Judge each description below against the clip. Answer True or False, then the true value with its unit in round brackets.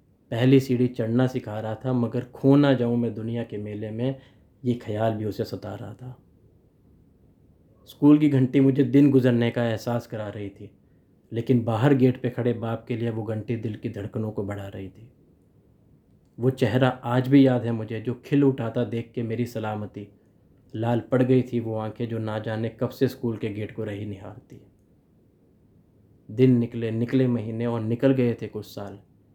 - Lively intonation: False (2.9 semitones)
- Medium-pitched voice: False (115 Hz)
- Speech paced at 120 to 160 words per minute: False (185 wpm)